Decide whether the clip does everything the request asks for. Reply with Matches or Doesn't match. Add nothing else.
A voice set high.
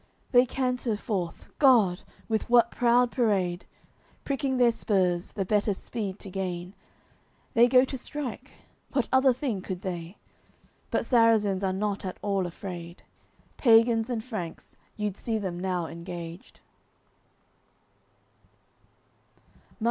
Matches